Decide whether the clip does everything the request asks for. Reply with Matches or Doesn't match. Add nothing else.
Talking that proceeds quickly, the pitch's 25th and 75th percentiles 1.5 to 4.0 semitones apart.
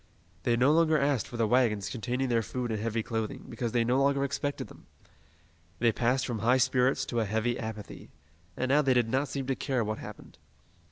Matches